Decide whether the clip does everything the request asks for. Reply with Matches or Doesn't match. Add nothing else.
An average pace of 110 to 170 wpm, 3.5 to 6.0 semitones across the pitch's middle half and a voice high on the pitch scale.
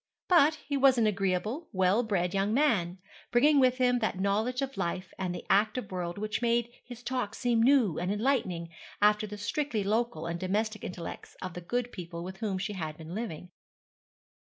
Doesn't match